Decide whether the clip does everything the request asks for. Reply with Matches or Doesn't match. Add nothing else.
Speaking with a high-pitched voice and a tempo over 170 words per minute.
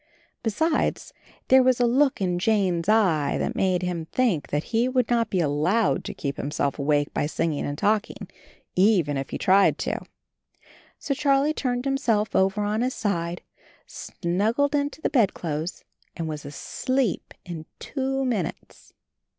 Doesn't match